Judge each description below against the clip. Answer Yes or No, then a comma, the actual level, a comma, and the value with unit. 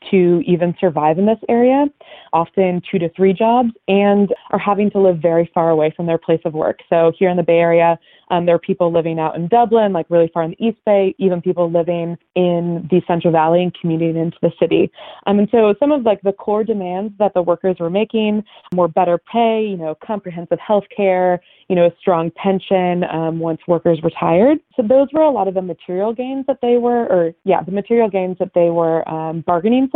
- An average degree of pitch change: Yes, average, 3.7 semitones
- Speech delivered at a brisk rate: Yes, fast, 220 wpm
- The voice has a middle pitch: Yes, medium, 180 Hz